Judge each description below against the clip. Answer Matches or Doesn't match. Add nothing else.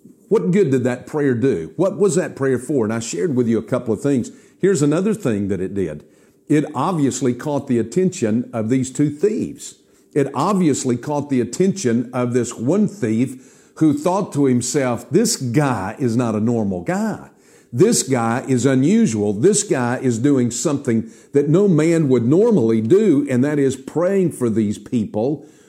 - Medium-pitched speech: Doesn't match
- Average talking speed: Matches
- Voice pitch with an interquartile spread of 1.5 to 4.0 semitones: Doesn't match